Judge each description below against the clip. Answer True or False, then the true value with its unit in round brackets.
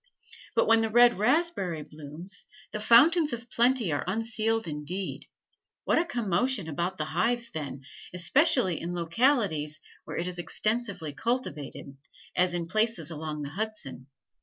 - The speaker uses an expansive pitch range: True (6.7 semitones)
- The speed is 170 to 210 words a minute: False (140 wpm)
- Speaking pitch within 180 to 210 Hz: True (190 Hz)